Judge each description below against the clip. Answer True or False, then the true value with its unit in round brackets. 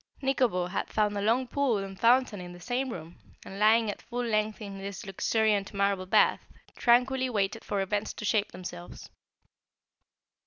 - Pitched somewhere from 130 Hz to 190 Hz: False (210 Hz)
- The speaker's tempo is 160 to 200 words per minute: True (165 wpm)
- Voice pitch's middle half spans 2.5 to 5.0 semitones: True (3.5 semitones)